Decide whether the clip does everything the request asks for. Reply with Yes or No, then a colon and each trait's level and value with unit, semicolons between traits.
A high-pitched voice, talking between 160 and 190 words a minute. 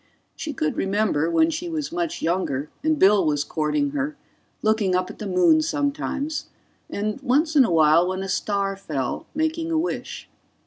Yes: high, 215 Hz; average, 175 wpm